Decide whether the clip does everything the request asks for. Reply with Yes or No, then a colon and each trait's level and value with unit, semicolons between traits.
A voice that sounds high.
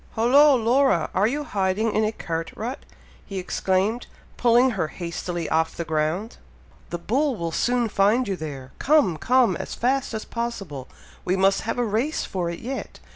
Yes: high, 215 Hz